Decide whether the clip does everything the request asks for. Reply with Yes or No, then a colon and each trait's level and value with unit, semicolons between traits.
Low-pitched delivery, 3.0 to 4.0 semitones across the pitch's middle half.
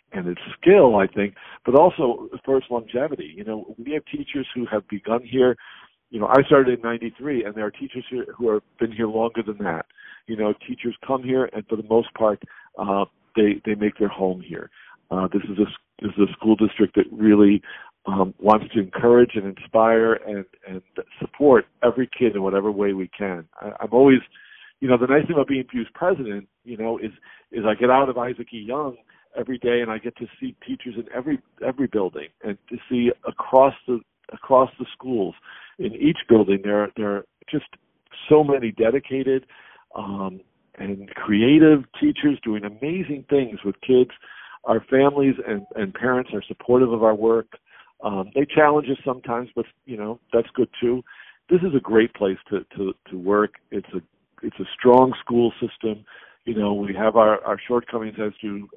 Yes: low, 115 Hz; average, 3.5 semitones